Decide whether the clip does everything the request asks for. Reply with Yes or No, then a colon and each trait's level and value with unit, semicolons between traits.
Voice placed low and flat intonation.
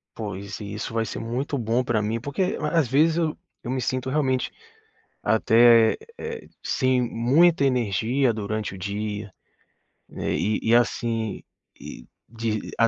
No: low, 115 Hz; average, 3.3 semitones